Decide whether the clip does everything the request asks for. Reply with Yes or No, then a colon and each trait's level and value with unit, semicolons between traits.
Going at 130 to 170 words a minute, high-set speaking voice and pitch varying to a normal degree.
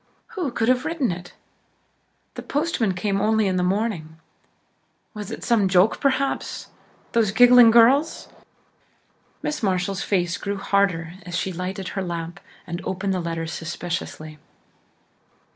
Yes: slow, 135 wpm; high, 195 Hz; average, 4.5 semitones